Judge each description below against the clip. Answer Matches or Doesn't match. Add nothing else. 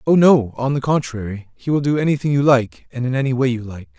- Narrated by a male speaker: Matches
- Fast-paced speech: Matches